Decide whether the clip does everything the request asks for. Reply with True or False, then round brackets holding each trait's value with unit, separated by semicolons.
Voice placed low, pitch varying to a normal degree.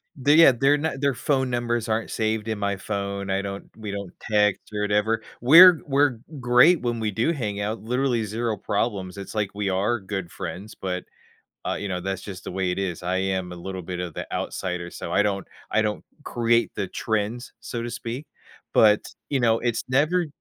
True (110 Hz; 3.7 semitones)